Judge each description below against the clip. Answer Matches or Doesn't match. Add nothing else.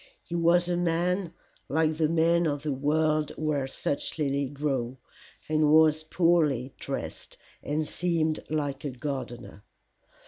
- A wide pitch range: Doesn't match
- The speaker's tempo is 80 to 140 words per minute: Matches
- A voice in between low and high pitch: Matches